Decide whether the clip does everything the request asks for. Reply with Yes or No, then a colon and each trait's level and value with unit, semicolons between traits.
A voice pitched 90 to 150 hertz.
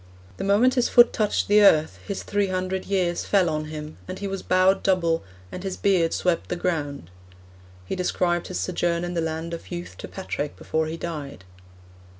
No: medium, 180 Hz